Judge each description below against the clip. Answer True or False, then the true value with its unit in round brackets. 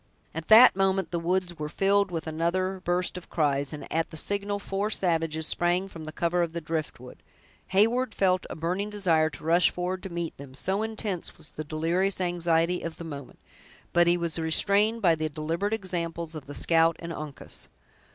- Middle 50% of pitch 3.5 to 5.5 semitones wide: False (3.0 semitones)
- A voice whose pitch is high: False (170 Hz)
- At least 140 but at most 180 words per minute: False (190 wpm)